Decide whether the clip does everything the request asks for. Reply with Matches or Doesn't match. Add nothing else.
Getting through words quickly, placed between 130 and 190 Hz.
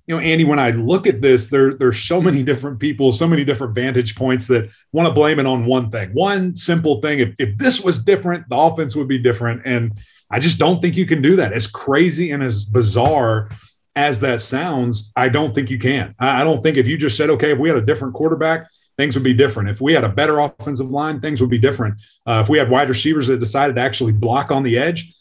Matches